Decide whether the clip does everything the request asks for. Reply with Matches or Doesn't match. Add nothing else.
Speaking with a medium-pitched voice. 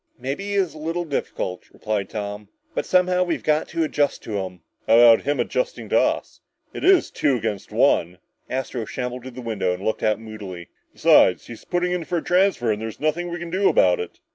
Doesn't match